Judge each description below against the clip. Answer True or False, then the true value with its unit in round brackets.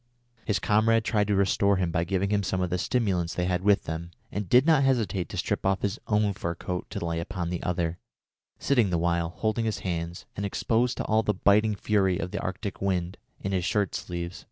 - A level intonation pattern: False (3.1 semitones)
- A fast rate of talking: True (225 wpm)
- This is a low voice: True (95 Hz)